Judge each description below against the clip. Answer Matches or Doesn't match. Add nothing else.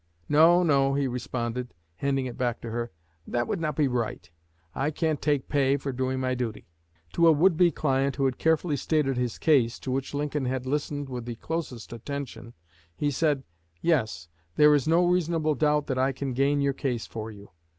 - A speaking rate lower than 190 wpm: Doesn't match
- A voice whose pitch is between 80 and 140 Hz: Matches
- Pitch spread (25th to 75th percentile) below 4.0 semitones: Matches